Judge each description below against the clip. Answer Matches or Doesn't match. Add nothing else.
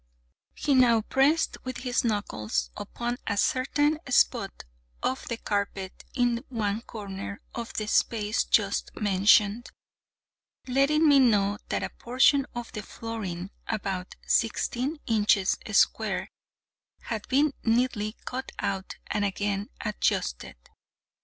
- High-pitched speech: Matches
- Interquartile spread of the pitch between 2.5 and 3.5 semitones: Doesn't match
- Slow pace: Matches